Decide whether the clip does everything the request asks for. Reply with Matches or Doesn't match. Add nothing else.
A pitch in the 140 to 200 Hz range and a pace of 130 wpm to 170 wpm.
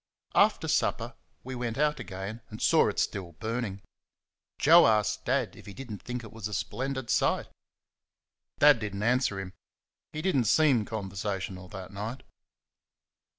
Doesn't match